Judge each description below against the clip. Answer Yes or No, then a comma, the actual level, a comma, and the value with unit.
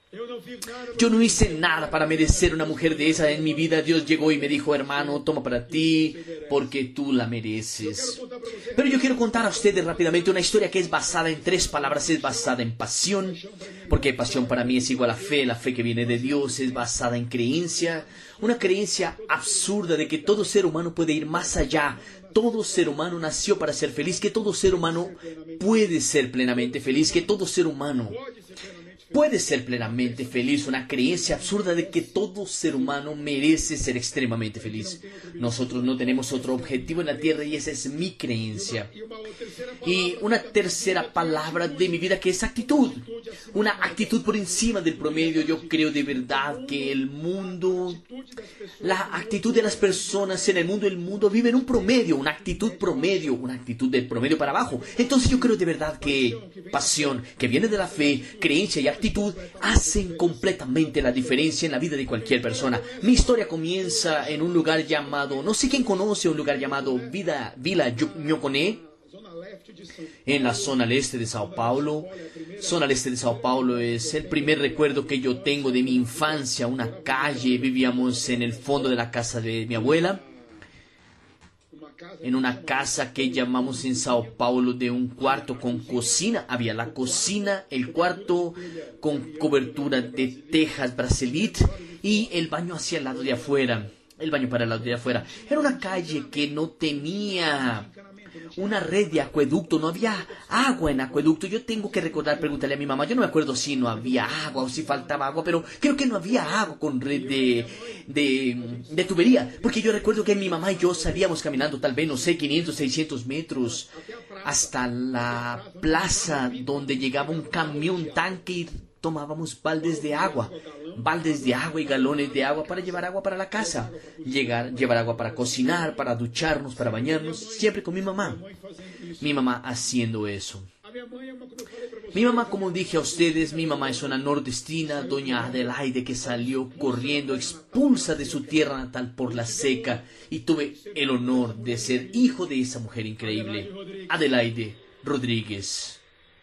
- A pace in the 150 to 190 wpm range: Yes, average, 175 wpm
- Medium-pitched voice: Yes, medium, 155 Hz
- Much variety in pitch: Yes, wide, 6.4 semitones